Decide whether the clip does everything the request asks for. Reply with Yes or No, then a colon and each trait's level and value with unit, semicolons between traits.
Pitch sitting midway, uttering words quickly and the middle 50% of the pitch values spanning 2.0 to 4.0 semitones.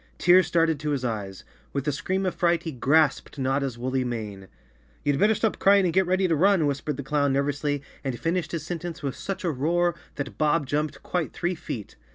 No: medium, 150 Hz; fast, 210 wpm; average, 4.4 semitones